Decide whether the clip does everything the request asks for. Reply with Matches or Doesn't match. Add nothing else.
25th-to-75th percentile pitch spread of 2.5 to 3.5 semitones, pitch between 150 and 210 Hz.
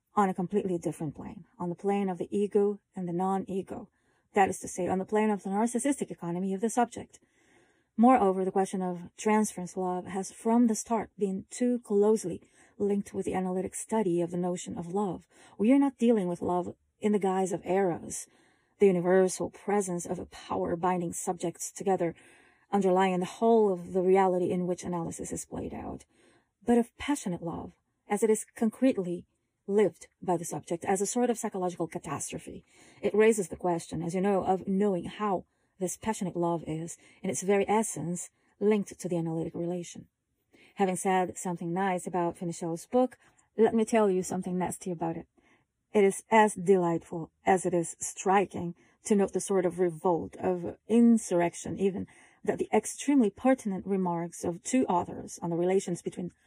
Matches